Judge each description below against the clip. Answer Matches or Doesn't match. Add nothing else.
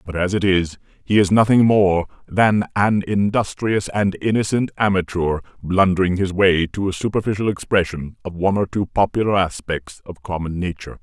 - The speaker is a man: Matches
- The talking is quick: Doesn't match